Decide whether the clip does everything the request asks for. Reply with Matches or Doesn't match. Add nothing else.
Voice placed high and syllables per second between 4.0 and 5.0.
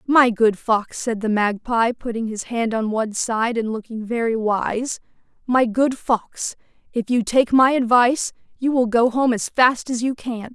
Matches